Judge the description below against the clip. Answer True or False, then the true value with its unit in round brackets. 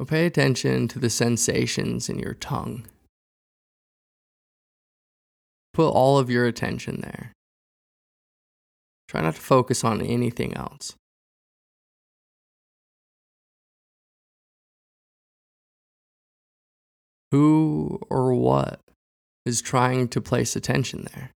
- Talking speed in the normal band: False (85 wpm)